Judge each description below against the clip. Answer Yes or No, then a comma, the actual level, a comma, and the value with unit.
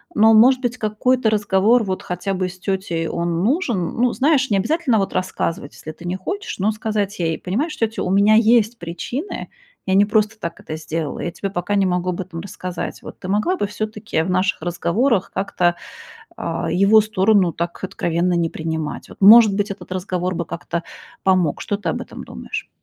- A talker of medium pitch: No, high, 195 Hz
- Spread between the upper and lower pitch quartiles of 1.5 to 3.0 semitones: No, average, 3.8 semitones